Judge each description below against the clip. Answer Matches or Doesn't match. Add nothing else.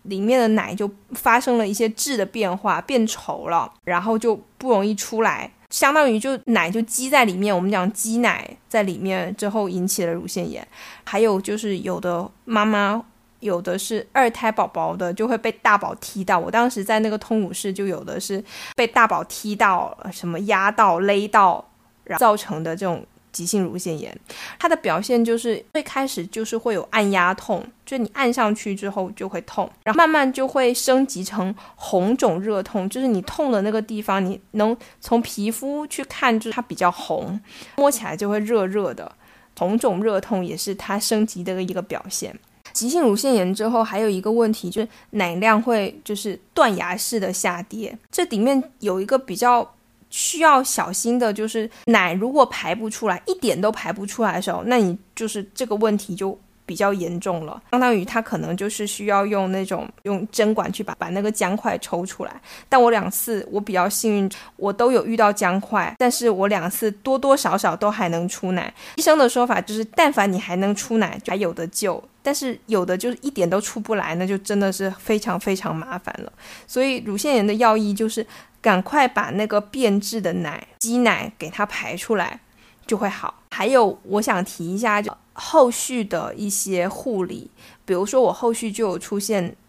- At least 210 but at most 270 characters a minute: Doesn't match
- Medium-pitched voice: Doesn't match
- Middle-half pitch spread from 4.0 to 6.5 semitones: Doesn't match